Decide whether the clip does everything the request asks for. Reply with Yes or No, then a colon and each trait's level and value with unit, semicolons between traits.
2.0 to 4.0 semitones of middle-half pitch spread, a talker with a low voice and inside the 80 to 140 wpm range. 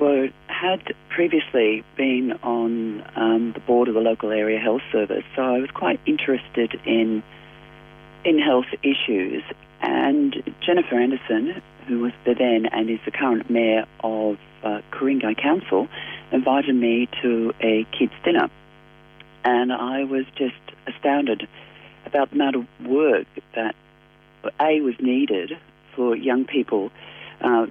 Yes: average, 3.4 semitones; low, 125 Hz; slow, 135 wpm